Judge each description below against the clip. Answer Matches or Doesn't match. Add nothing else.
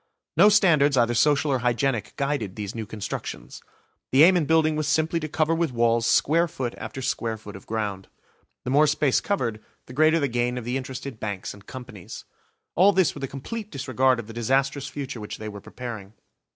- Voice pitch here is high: Doesn't match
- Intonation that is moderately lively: Matches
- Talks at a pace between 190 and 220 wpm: Matches